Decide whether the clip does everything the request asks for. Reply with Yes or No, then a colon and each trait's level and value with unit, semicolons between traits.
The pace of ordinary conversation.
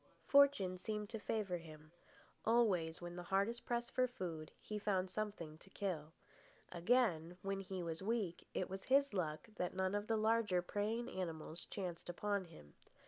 Yes: average, 160 wpm